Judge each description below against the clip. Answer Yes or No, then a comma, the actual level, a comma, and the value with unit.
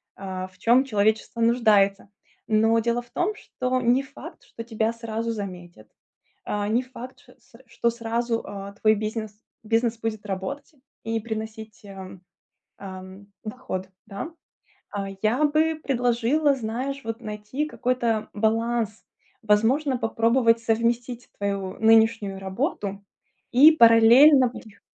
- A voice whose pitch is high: Yes, high, 225 Hz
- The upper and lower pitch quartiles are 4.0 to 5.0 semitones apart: No, average, 2.8 semitones